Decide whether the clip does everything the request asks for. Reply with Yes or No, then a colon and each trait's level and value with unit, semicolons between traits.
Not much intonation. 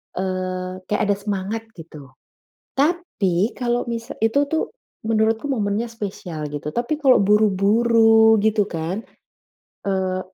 No: average, 3.5 semitones